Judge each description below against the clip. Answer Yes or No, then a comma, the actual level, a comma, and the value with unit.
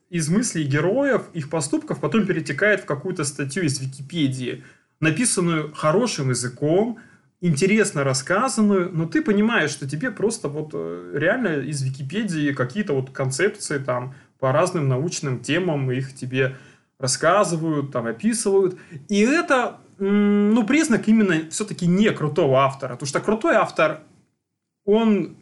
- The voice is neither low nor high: Yes, medium, 165 Hz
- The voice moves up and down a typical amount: No, wide, 6.9 semitones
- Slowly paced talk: No, average, 125 wpm